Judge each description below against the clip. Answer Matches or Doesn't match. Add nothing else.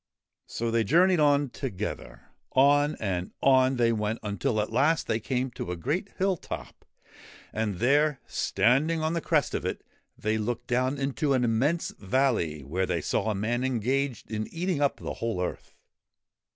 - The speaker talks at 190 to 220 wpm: Doesn't match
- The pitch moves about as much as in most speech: Matches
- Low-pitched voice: Matches